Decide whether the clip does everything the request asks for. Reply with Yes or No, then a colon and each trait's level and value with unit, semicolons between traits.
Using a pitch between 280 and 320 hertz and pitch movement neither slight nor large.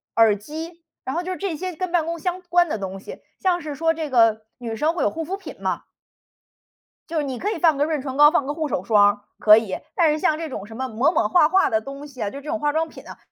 No: very high, 300 Hz; wide, 6.0 semitones